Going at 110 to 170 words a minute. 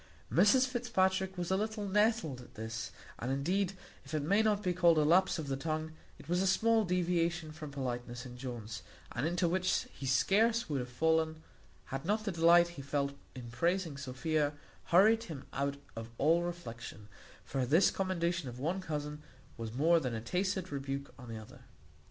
No: average, 185 wpm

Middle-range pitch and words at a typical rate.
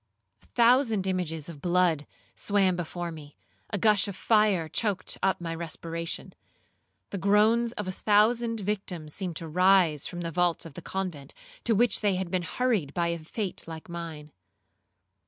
Yes: medium, 180 Hz; average, 160 wpm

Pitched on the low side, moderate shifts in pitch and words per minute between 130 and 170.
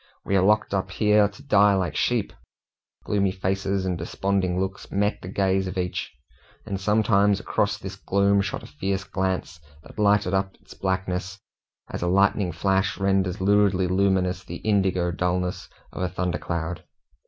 No: very low, 95 Hz; narrow, 1.6 semitones; average, 165 wpm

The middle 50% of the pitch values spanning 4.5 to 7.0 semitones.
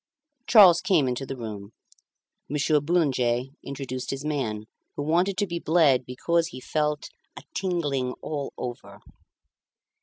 Yes: average, 5.0 semitones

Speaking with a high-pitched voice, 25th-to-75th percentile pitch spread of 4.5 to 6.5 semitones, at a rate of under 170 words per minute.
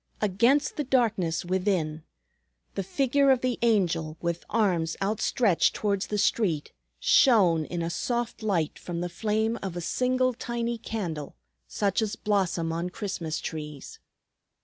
Yes: high, 200 Hz; wide, 5.5 semitones; average, 140 wpm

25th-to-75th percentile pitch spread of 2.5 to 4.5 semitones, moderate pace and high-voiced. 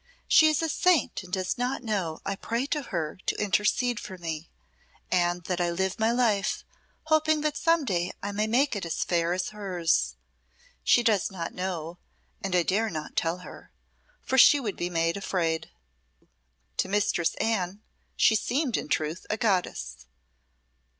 No: average, 5.2 semitones; average, 170 wpm; high, 195 Hz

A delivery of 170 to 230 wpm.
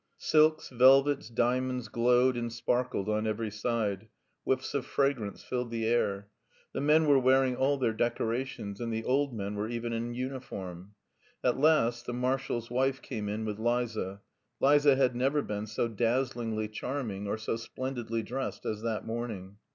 No: average, 160 wpm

